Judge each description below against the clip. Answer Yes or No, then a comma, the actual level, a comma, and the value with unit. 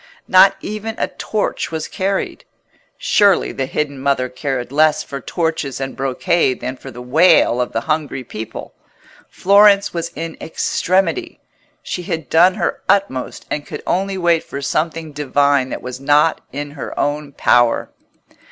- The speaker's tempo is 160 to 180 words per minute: No, average, 150 wpm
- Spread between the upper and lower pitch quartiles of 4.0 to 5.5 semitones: Yes, average, 5.1 semitones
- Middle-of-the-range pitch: Yes, medium, 150 Hz